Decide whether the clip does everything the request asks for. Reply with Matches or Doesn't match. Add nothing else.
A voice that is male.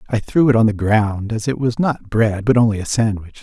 Matches